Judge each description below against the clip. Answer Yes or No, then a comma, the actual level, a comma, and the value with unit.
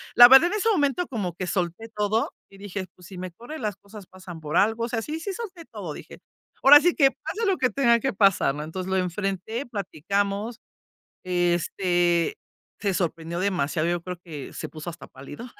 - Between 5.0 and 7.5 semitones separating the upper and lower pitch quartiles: Yes, wide, 5.5 semitones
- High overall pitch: Yes, high, 195 Hz